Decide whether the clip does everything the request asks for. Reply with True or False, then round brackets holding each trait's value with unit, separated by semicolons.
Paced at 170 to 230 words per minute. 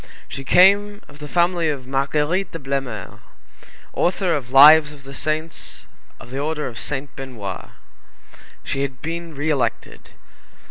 False (145 wpm)